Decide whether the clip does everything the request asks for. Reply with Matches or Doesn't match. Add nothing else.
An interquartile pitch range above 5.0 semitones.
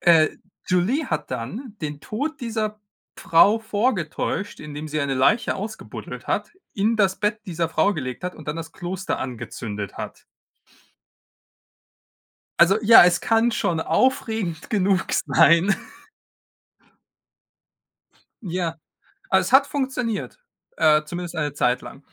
Matches